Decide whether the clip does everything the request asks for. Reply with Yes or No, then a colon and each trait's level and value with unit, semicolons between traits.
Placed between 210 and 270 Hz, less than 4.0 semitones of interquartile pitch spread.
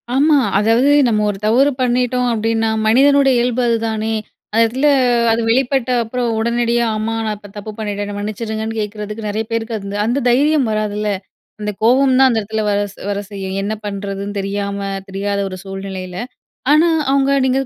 Yes: high, 220 Hz; average, 3.3 semitones